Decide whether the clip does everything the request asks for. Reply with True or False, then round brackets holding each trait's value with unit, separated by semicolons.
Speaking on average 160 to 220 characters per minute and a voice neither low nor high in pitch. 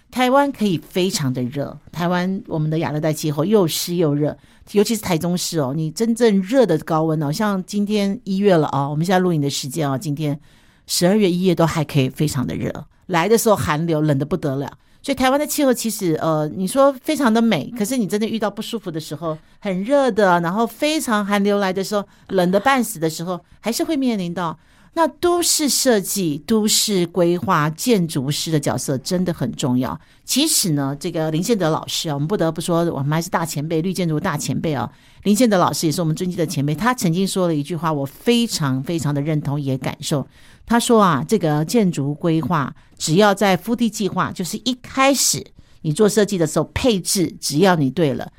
False (315 characters per minute; 175 Hz)